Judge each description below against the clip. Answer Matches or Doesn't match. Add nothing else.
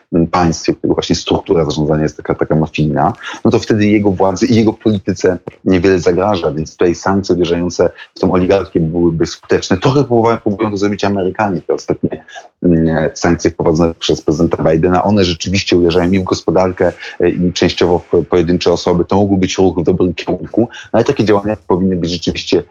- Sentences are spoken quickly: Matches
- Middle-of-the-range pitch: Doesn't match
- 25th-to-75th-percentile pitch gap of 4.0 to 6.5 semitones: Doesn't match